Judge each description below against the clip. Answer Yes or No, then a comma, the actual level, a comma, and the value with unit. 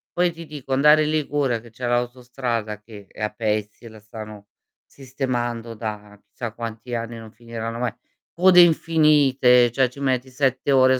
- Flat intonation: No, average, 3.2 semitones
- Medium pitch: No, low, 120 Hz